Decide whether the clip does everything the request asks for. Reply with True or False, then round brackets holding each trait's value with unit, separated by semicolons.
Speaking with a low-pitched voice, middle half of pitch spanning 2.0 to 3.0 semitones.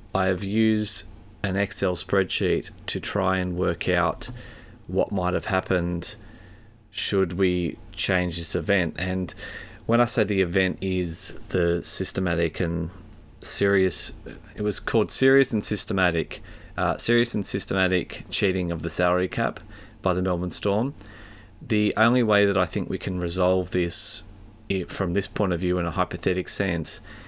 True (95 Hz; 2.4 semitones)